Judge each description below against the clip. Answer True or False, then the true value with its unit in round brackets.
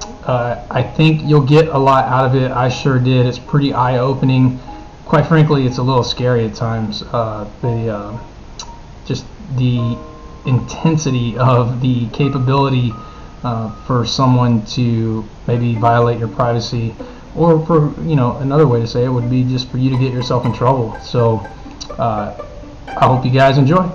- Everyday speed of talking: True (170 wpm)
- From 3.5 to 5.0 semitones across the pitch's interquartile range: False (2.4 semitones)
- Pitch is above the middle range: False (125 Hz)